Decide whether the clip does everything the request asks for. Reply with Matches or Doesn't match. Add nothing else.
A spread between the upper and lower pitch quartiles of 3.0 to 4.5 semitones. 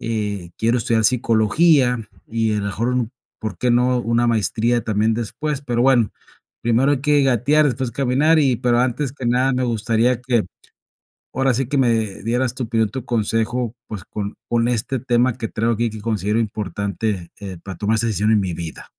Doesn't match